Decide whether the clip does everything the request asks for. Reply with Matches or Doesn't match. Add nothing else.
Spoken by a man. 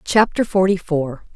Doesn't match